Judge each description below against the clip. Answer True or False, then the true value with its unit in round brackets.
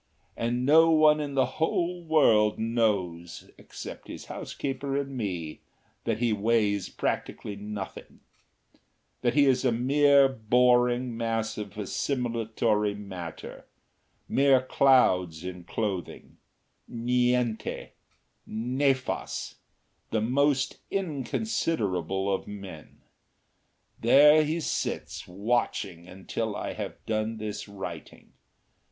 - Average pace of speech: False (100 wpm)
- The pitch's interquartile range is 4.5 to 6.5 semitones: True (4.8 semitones)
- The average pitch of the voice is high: False (115 Hz)